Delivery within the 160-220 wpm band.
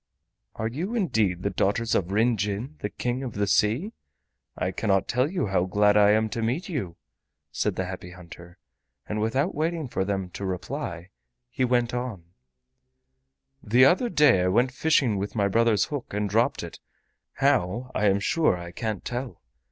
Yes: average, 175 wpm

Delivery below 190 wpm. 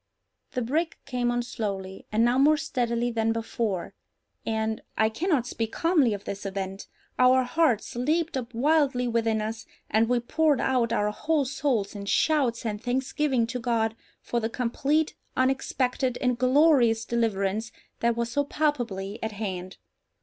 Yes: average, 150 wpm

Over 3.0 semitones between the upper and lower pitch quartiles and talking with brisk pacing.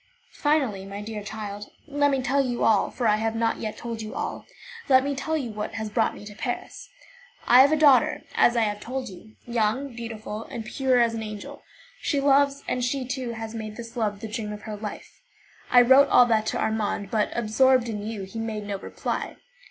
Yes: average, 3.4 semitones; fast, 215 wpm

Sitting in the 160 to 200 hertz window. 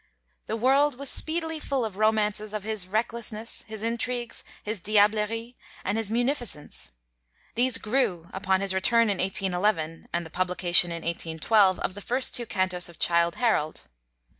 No: high, 210 Hz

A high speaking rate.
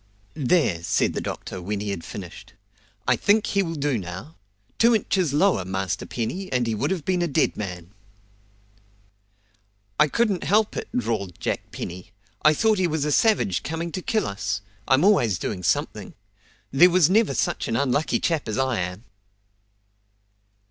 No: average, 170 wpm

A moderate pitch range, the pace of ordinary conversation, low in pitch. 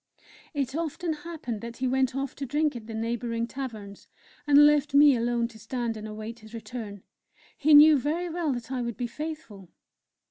No: average, 4.3 semitones; average, 185 wpm; very high, 250 Hz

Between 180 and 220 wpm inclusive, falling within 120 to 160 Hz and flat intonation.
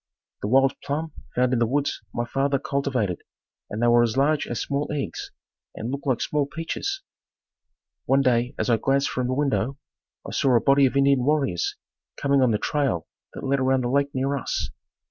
Yes: average, 195 wpm; low, 135 Hz; narrow, 2.3 semitones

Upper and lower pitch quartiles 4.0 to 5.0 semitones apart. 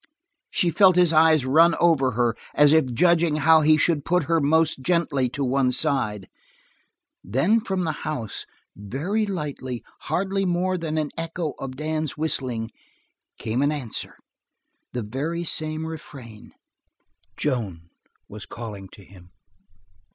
Yes: average, 4.7 semitones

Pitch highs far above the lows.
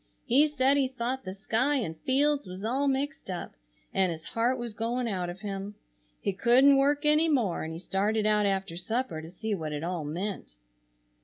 Yes: wide, 6.0 semitones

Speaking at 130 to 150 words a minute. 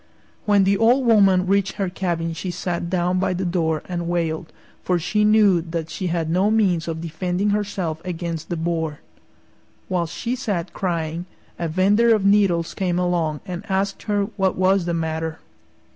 No: average, 175 wpm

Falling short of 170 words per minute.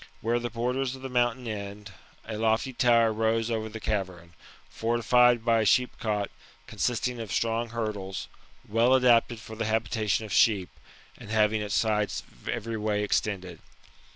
Yes: average, 155 wpm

